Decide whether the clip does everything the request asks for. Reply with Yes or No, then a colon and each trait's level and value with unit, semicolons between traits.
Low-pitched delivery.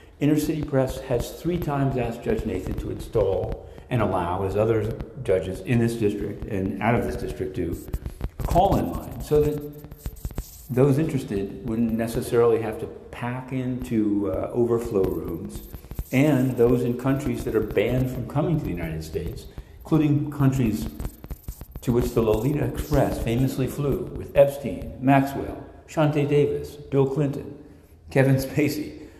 Yes: low, 125 Hz